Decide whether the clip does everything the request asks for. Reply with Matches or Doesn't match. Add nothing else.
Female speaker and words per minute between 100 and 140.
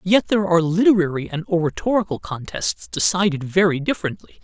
Doesn't match